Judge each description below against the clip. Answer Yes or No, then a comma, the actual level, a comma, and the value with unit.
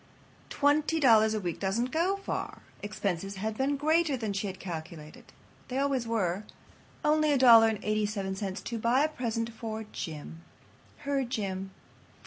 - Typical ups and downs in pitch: No, wide, 5.8 semitones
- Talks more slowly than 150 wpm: Yes, slow, 135 wpm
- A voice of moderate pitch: No, high, 225 Hz